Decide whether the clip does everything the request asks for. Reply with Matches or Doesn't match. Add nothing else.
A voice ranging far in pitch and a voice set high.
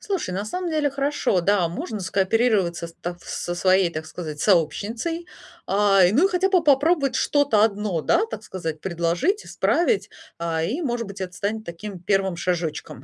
Matches